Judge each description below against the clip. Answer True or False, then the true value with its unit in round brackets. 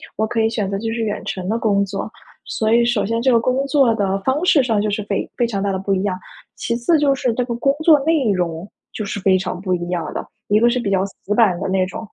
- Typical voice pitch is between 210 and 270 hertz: True (215 Hz)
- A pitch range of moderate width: True (3.5 semitones)